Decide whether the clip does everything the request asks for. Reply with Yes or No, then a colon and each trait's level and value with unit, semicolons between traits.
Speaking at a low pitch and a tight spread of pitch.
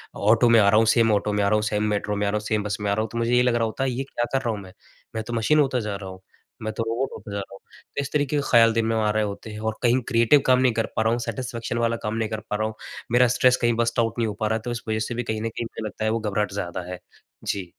Yes: low, 115 Hz; narrow, 2.0 semitones